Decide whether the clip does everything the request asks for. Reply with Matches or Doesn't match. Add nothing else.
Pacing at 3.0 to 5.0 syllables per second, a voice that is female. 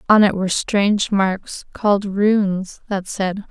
Matches